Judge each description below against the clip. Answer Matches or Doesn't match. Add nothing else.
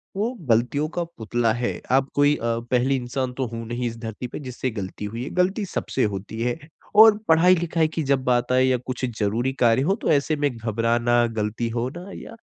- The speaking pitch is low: Matches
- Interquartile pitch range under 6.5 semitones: Matches